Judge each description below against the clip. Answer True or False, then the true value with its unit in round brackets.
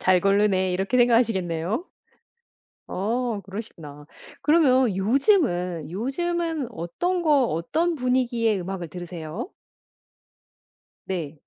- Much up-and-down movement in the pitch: True (6.5 semitones)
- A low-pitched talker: False (210 Hz)